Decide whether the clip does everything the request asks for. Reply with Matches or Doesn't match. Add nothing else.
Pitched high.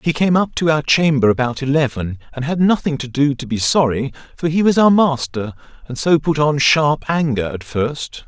Doesn't match